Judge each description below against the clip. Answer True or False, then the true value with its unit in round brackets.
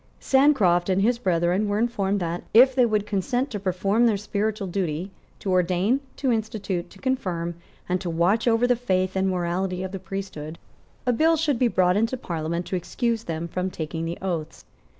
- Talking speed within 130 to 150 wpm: False (190 wpm)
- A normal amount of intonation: True (4.4 semitones)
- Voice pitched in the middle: False (195 Hz)